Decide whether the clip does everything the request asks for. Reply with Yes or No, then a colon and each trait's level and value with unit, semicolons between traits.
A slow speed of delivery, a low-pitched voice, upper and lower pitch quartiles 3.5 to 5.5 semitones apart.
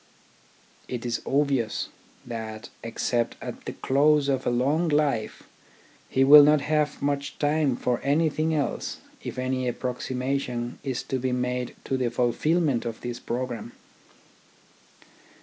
No: slow, 130 wpm; low, 130 Hz; average, 3.1 semitones